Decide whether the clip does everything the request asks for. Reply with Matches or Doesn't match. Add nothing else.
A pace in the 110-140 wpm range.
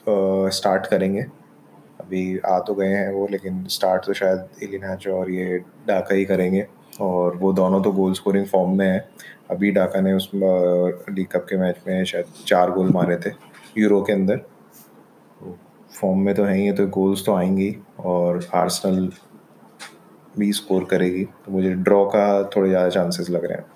Doesn't match